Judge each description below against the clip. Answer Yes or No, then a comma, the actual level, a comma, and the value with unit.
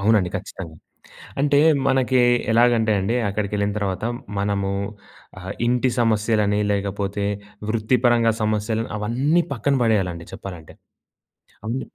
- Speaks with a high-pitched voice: No, low, 110 Hz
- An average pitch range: Yes, average, 3.0 semitones